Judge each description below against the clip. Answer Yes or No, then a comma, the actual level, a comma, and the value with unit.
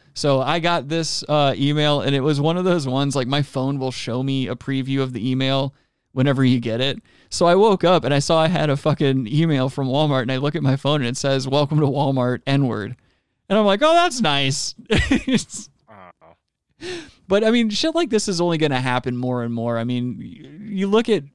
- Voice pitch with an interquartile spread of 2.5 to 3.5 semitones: No, average, 4.6 semitones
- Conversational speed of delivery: No, fast, 230 wpm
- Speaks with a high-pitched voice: No, medium, 140 Hz